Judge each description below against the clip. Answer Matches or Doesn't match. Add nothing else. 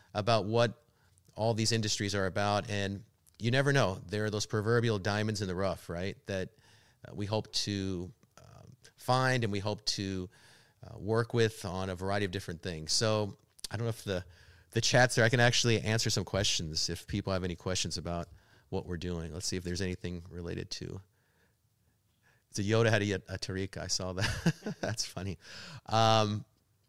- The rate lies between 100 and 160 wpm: Doesn't match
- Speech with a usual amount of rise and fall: Matches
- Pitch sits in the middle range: Doesn't match